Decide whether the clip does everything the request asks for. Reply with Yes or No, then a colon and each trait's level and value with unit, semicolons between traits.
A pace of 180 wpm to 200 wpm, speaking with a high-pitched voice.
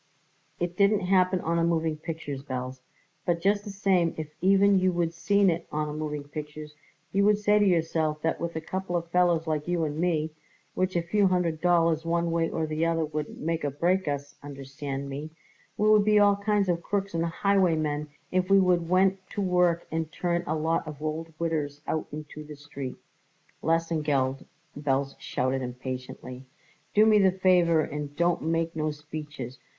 No: average, 185 wpm; medium, 165 Hz